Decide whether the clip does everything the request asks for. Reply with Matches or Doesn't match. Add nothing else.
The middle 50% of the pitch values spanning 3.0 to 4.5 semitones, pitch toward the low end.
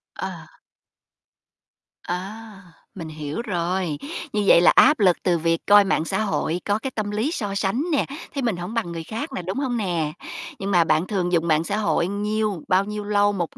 Doesn't match